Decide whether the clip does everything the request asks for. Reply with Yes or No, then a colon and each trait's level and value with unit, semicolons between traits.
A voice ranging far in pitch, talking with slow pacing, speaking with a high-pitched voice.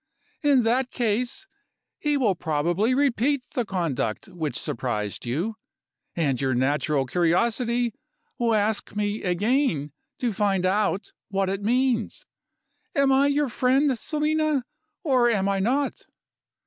Yes: wide, 6.7 semitones; slow, 125 wpm; high, 220 Hz